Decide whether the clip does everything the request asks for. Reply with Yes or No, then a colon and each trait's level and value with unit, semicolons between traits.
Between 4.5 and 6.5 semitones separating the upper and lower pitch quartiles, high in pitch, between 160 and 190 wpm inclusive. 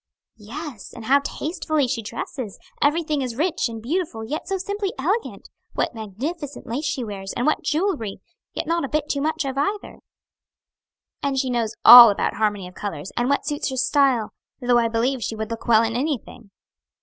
Yes: average, 5.1 semitones; very high, 260 Hz; average, 185 wpm